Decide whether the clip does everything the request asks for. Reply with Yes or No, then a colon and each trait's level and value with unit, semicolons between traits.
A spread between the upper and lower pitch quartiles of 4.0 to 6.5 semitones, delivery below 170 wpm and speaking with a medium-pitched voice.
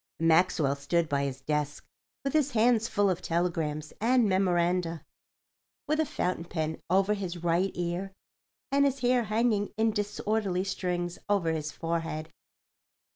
Yes: average, 4.5 semitones; average, 140 wpm; medium, 180 Hz